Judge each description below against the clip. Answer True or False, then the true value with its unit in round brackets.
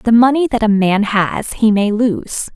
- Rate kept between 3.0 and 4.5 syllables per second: True (4.0 syllables/s)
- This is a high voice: True (215 Hz)